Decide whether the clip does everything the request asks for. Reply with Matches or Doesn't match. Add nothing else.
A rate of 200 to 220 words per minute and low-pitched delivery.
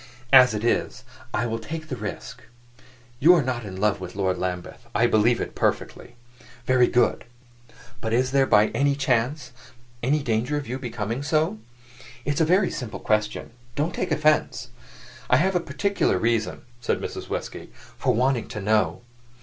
Doesn't match